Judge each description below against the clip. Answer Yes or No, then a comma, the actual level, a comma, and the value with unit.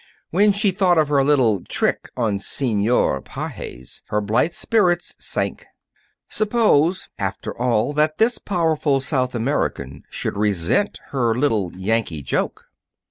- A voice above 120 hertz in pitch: Yes, low, 135 Hz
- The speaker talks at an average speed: No, slow, 130 wpm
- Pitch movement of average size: No, wide, 8.5 semitones